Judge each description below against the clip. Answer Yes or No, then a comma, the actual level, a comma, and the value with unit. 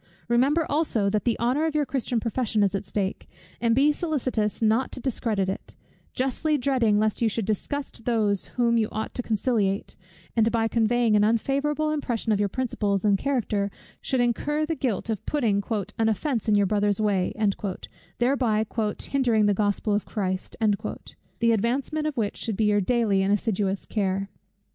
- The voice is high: Yes, high, 225 Hz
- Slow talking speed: No, average, 170 wpm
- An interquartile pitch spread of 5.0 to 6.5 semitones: No, average, 3.8 semitones